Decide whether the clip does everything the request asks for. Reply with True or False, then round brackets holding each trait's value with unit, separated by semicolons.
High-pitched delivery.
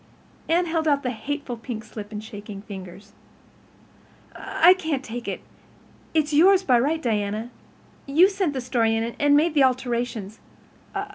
True (250 Hz)